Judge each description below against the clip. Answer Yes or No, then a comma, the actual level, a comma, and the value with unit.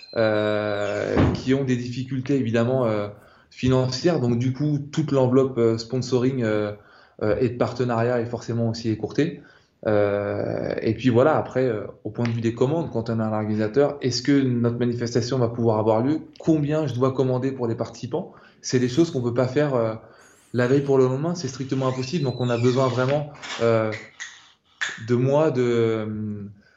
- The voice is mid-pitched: No, low, 125 Hz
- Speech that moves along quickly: No, average, 185 wpm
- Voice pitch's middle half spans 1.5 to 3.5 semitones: Yes, average, 2.9 semitones